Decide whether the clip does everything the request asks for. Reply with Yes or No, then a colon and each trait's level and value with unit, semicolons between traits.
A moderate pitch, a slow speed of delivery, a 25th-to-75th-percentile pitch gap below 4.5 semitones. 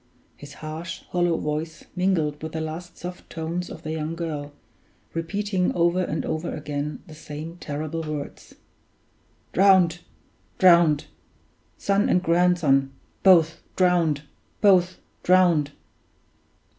Yes: medium, 165 Hz; slow, 115 wpm; average, 2.7 semitones